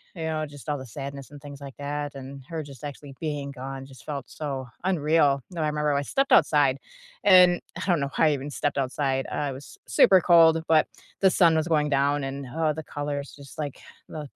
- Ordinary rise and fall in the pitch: No, narrow, 2.3 semitones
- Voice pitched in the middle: Yes, medium, 145 Hz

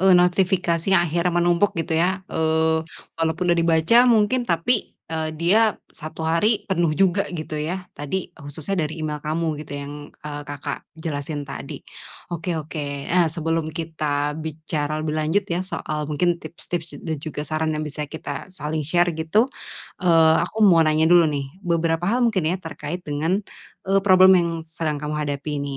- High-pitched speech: No, medium, 160 Hz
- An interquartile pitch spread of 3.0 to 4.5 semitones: No, narrow, 2.6 semitones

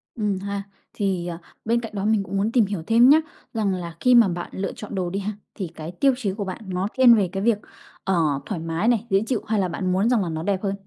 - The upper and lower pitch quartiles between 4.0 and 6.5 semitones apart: No, average, 3.1 semitones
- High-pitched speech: Yes, high, 200 Hz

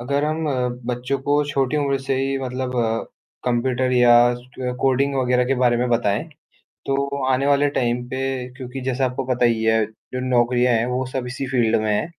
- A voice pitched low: Yes, low, 125 Hz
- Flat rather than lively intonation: Yes, narrow, 1.8 semitones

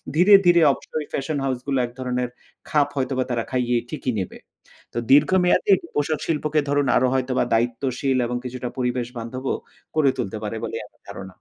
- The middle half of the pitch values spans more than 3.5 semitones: No, average, 2.7 semitones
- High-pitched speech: No, low, 130 Hz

